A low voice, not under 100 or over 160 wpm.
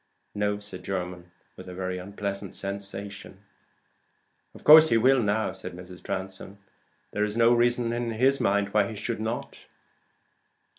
Yes: low, 100 Hz; average, 150 wpm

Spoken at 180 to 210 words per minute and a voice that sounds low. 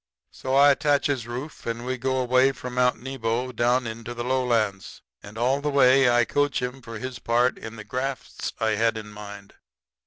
Yes: average, 190 wpm; low, 125 Hz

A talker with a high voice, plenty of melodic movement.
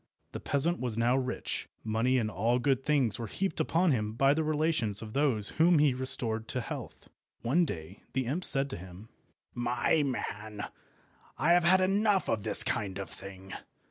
No: low, 125 Hz; wide, 5.9 semitones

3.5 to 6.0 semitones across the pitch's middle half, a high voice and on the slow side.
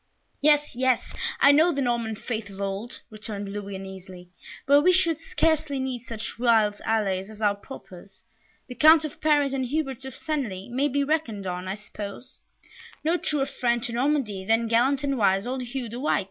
No: wide, 5.4 semitones; high, 240 Hz; average, 185 wpm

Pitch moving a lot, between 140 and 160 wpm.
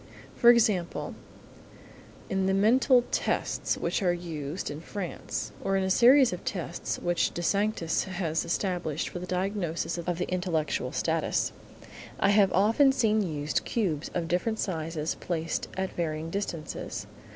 No: average, 3.5 semitones; average, 145 wpm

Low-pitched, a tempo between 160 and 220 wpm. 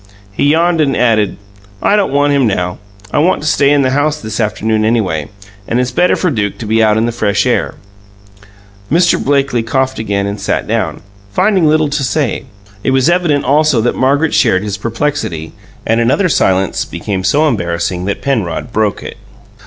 Yes: low, 125 Hz; average, 185 wpm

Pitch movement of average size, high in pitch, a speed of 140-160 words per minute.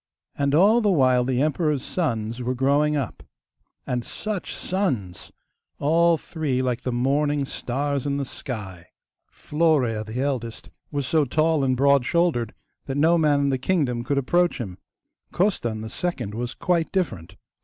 No: average, 4.5 semitones; medium, 140 Hz; average, 155 wpm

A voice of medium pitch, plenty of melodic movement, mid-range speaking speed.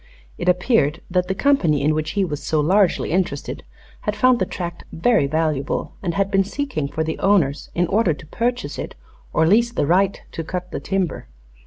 No: medium, 180 Hz; average, 4.4 semitones; average, 195 wpm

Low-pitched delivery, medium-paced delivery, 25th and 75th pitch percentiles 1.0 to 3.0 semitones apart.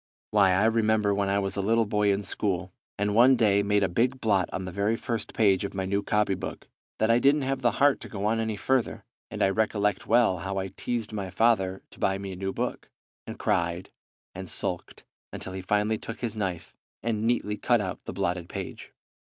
No: low, 105 Hz; fast, 220 wpm; average, 2.7 semitones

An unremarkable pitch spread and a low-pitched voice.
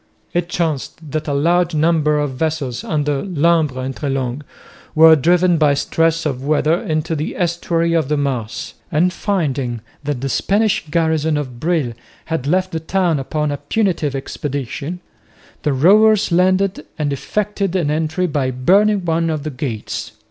No: average, 3.4 semitones; medium, 155 Hz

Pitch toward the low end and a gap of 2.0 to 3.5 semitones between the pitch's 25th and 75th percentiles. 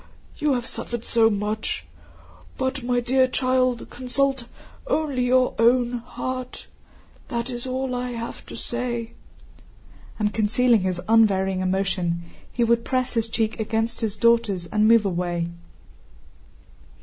No: high, 235 Hz; average, 3.0 semitones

